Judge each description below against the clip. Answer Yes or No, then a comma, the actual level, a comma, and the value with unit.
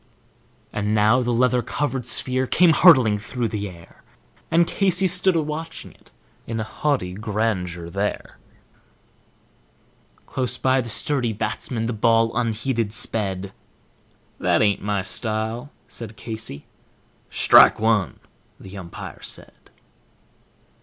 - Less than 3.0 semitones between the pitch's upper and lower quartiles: No, average, 3.8 semitones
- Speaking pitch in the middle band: No, low, 115 Hz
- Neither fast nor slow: No, slow, 120 wpm